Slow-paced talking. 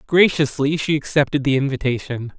Yes: slow, 125 wpm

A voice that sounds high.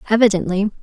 Yes: high, 205 Hz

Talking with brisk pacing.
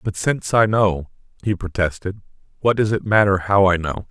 No: average, 190 wpm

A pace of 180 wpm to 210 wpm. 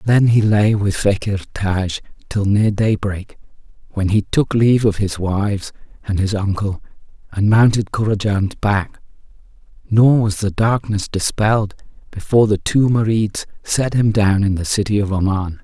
No: average, 155 wpm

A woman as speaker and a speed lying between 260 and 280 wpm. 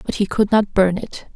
Yes: female; fast, 265 wpm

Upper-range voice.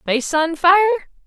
Yes: very high, 340 Hz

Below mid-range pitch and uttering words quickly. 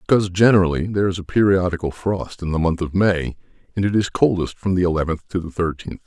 Yes: very low, 90 Hz; fast, 220 wpm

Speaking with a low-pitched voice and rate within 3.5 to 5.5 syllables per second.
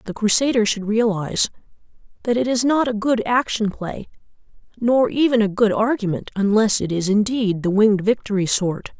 No: high, 215 Hz; 5.2 syllables/s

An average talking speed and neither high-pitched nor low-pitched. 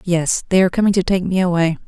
No: fast, 255 wpm; medium, 180 Hz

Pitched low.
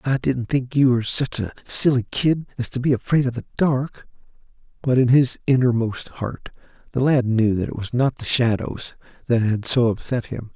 Yes: low, 125 Hz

